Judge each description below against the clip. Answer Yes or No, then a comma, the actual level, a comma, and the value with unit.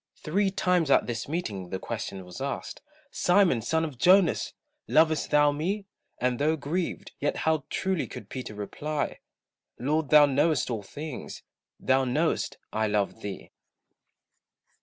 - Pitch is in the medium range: Yes, medium, 145 Hz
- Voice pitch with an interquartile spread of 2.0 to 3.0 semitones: No, average, 5.1 semitones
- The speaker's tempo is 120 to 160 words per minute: Yes, average, 140 wpm